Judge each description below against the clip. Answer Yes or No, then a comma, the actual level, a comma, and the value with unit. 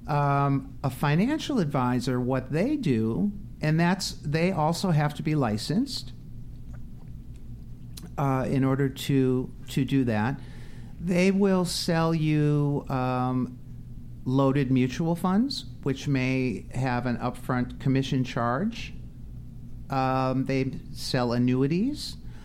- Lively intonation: No, average, 3.6 semitones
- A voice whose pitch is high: No, low, 135 Hz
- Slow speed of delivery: Yes, slow, 110 wpm